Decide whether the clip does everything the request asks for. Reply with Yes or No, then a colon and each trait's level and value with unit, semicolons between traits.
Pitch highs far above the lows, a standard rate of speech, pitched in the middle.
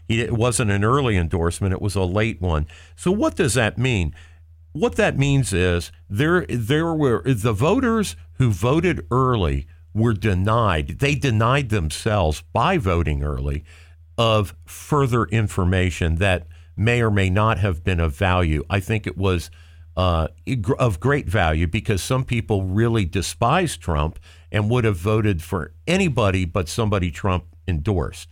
No: wide, 6.1 semitones; average, 150 wpm; low, 100 Hz